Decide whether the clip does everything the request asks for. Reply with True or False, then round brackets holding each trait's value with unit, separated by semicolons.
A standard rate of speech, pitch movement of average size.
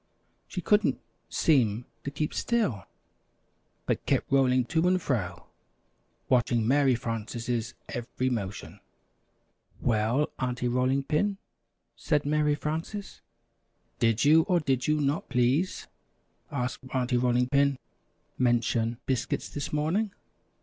False (115 wpm; 4.0 semitones)